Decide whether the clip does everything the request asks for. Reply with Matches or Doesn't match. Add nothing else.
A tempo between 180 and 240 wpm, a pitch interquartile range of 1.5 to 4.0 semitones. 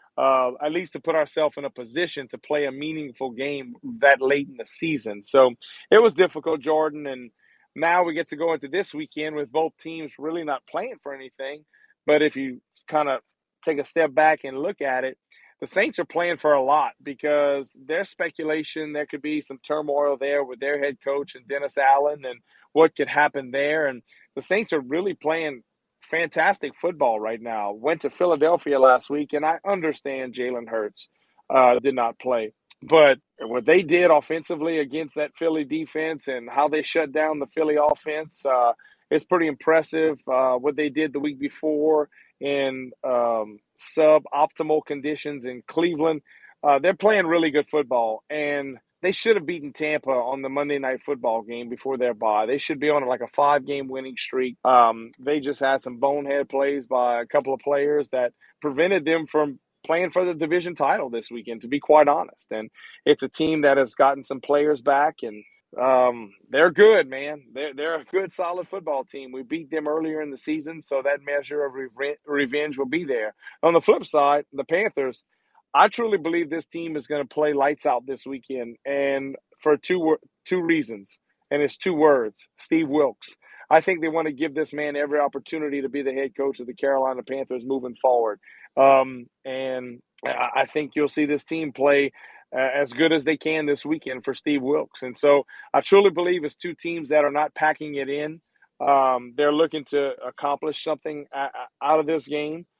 Matches